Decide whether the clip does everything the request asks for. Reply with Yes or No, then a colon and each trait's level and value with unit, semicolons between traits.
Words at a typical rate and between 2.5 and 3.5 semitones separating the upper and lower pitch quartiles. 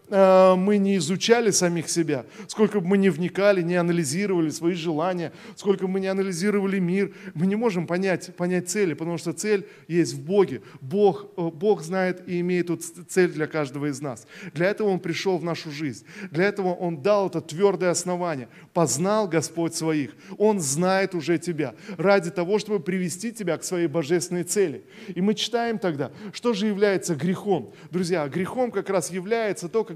No: fast, 175 wpm; average, 3.0 semitones